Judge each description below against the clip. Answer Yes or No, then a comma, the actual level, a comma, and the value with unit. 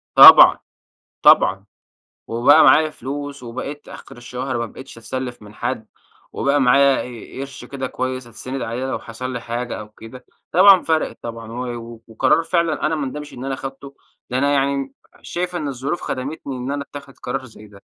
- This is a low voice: Yes, low, 130 Hz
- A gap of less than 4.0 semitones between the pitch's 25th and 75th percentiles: Yes, average, 2.9 semitones